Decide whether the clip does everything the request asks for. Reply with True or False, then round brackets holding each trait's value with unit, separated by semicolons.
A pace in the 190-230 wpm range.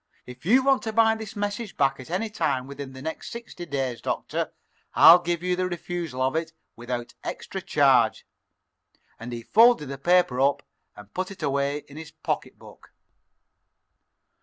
False (165 wpm)